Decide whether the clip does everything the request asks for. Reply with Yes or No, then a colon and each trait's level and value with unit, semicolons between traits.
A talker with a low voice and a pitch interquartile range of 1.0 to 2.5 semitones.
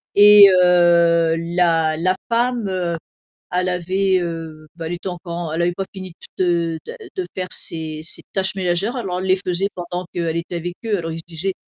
No: medium, 175 Hz; narrow, 2.0 semitones